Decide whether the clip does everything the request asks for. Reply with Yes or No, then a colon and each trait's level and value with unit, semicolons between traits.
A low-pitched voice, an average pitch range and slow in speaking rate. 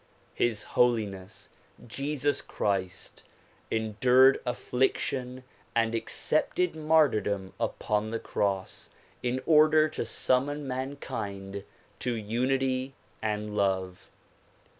Yes: low, 120 Hz; average, 4.5 semitones; slow, 90 wpm